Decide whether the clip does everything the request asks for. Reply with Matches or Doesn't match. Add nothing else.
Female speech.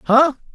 Doesn't match